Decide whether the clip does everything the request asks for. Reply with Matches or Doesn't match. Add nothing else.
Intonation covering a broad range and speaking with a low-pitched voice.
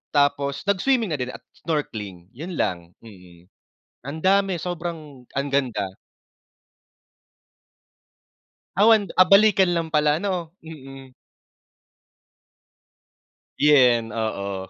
Doesn't match